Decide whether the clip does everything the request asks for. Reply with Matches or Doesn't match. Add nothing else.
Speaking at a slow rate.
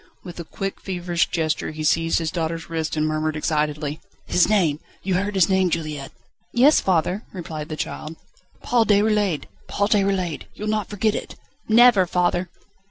Doesn't match